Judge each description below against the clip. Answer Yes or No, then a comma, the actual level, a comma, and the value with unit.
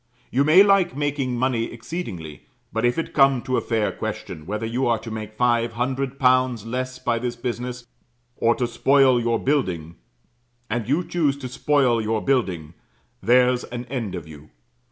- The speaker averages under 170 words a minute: No, average, 175 wpm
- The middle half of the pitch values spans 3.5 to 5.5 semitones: No, average, 2.8 semitones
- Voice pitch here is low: Yes, low, 125 Hz